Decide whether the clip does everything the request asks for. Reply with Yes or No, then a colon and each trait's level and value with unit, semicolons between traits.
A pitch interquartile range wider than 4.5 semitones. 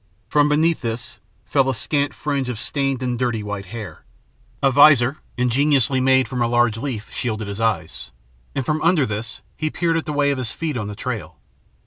No: average, 4.1 semitones